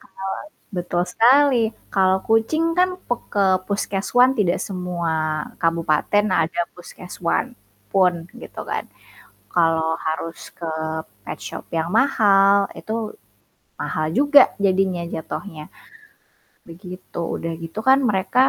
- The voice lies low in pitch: No, high, 190 Hz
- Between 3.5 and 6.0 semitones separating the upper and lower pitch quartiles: Yes, average, 4.2 semitones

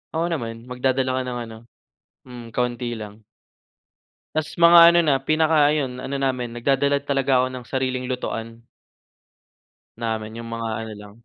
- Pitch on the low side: Yes, low, 125 Hz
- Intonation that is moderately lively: Yes, average, 3.2 semitones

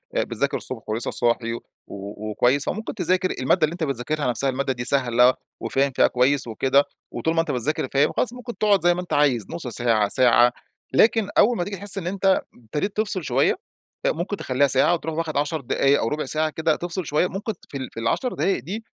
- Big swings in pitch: Yes, wide, 6.3 semitones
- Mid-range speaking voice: Yes, medium, 150 Hz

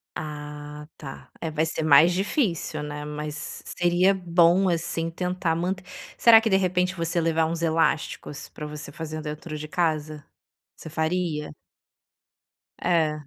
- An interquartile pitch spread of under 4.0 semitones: Yes, average, 2.7 semitones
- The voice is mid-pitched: Yes, medium, 160 Hz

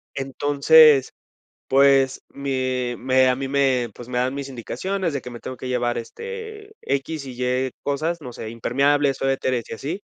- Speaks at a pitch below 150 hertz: Yes, low, 135 Hz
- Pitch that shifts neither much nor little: No, narrow, 2.2 semitones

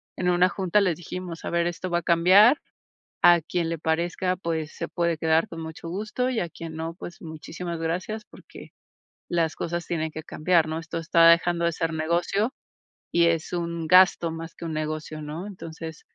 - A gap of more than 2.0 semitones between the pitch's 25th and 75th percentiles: No, narrow, 1.6 semitones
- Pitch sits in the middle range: Yes, medium, 170 Hz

